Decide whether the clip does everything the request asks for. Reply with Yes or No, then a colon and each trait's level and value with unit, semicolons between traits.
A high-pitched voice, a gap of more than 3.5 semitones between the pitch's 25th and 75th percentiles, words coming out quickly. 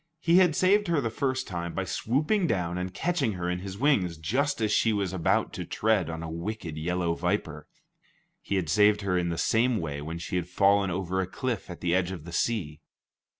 No: very low, 95 Hz; average, 5.2 semitones; fast, 220 wpm